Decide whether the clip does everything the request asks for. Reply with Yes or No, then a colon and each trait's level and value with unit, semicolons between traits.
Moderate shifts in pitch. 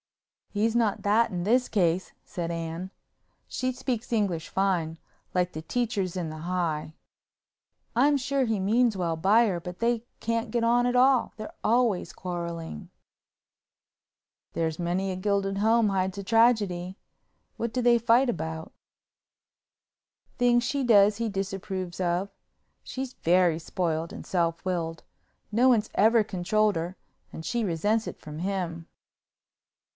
Yes: average, 4.9 semitones